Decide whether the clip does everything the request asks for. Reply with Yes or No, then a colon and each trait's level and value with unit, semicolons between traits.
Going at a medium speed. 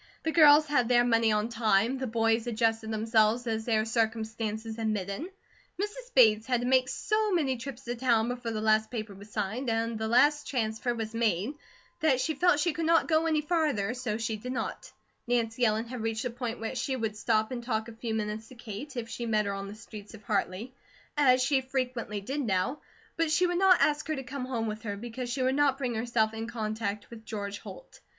No: fast, 220 wpm